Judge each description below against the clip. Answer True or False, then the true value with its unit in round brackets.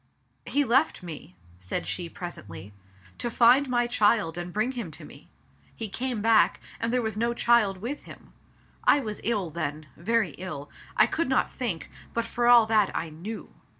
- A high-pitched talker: True (220 Hz)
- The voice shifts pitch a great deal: True (5.7 semitones)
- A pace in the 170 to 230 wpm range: True (190 wpm)